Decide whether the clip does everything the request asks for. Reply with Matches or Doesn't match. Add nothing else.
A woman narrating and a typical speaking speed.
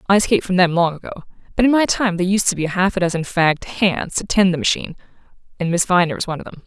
Doesn't match